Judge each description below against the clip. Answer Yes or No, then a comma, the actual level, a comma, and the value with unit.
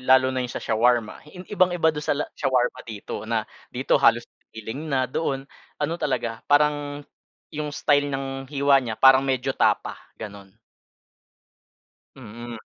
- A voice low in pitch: Yes, low, 130 Hz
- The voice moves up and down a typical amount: Yes, average, 3.5 semitones